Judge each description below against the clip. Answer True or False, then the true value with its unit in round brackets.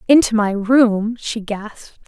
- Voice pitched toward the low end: False (220 Hz)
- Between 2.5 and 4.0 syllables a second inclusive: True (3.9 syllables/s)